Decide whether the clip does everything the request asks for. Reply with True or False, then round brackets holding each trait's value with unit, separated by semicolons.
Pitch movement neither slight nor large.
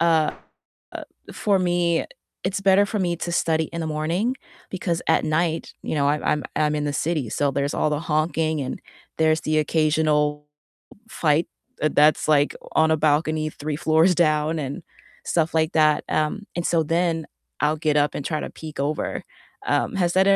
False (2.0 semitones)